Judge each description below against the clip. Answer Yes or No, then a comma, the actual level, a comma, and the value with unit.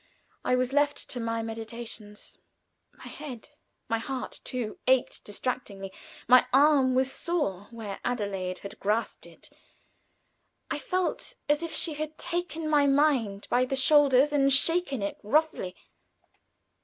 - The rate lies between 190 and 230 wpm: No, slow, 135 wpm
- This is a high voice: Yes, very high, 255 Hz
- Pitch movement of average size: Yes, average, 4.8 semitones